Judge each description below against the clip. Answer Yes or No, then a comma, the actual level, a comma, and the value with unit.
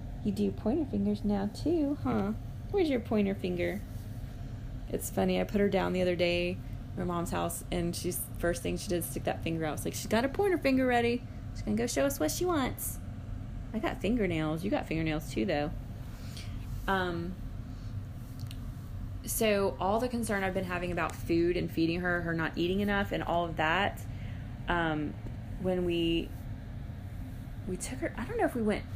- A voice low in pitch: Yes, low, 120 Hz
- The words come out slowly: No, average, 190 wpm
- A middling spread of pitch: No, wide, 9.0 semitones